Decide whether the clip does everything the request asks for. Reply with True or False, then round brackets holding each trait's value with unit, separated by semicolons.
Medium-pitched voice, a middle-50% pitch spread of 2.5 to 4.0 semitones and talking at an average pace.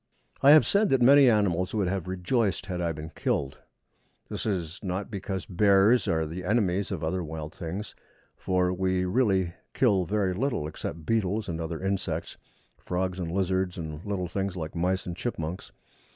False (95 Hz; 2.9 semitones; 170 wpm)